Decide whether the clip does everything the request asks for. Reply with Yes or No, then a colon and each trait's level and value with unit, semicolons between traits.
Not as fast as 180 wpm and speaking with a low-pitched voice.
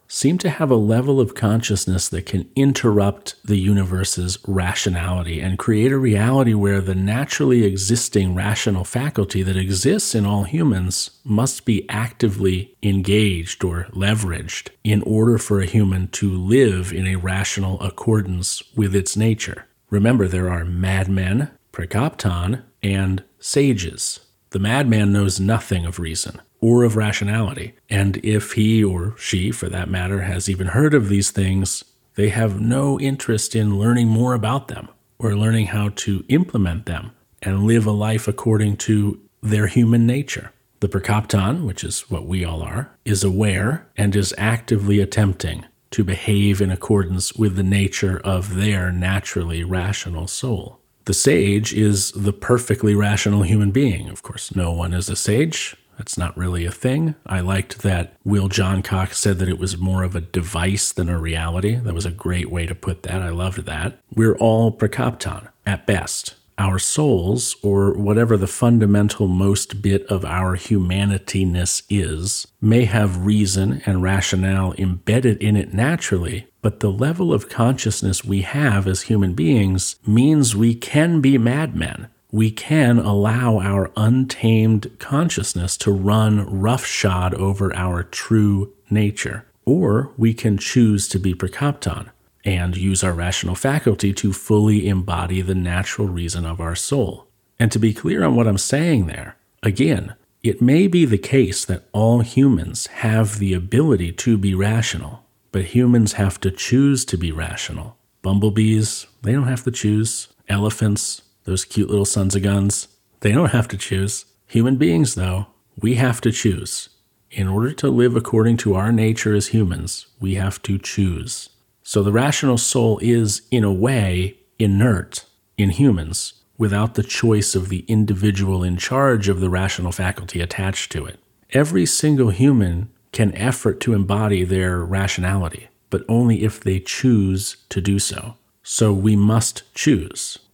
Yes: average, 155 wpm; low, 105 Hz